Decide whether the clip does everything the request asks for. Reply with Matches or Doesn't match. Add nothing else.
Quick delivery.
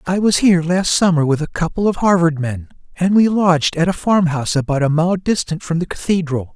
Matches